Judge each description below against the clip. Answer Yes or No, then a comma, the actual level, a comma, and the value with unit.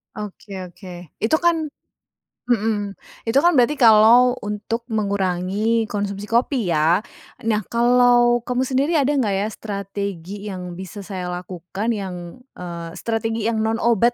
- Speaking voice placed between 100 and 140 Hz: No, high, 210 Hz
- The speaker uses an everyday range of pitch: Yes, average, 3.7 semitones